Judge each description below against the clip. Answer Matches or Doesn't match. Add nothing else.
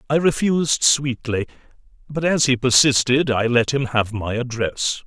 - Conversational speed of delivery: Matches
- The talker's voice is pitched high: Doesn't match